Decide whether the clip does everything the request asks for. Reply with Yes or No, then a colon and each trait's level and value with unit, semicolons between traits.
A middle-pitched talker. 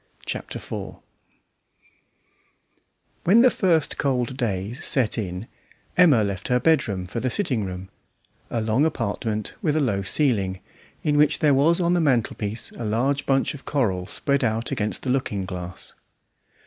No: low, 125 Hz